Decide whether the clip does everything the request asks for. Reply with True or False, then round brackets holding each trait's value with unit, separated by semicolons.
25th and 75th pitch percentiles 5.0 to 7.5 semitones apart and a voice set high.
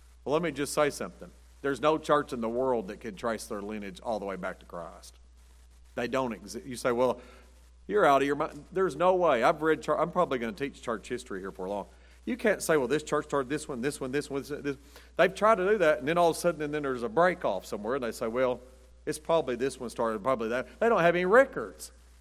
False (5.5 semitones; 135 Hz)